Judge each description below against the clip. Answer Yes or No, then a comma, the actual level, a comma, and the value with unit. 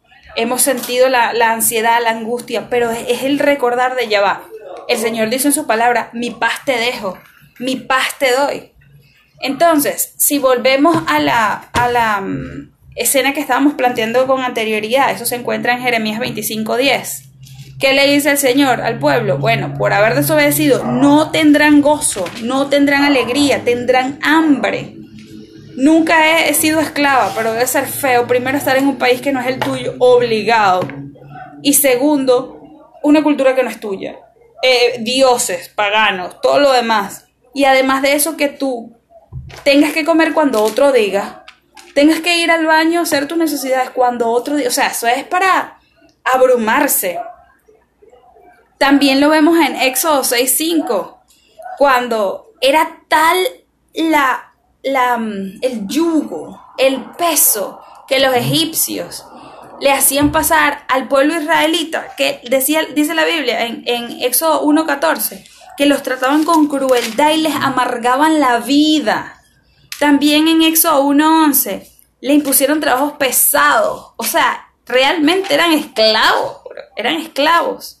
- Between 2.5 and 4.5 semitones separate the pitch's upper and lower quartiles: Yes, average, 3.9 semitones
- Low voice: No, very high, 270 Hz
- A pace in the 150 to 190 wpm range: No, average, 140 wpm